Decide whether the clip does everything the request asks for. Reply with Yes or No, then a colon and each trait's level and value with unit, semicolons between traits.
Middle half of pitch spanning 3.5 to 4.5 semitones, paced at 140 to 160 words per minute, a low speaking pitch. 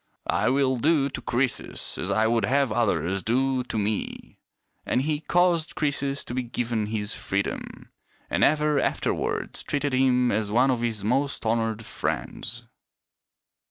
Yes: average, 4.1 semitones; average, 150 wpm; low, 125 Hz